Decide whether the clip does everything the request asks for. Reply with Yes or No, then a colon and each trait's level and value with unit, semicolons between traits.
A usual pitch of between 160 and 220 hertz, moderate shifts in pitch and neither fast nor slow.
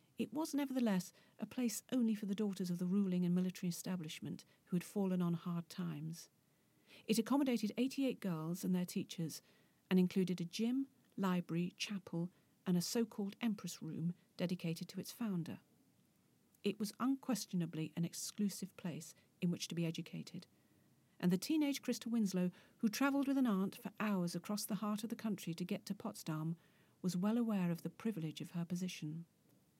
Yes: medium, 185 Hz; average, 4.1 semitones; average, 175 wpm